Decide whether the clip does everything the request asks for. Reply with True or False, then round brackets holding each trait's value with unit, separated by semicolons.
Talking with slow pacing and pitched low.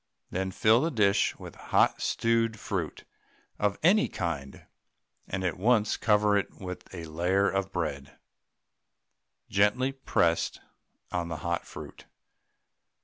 True (125 wpm; 95 Hz)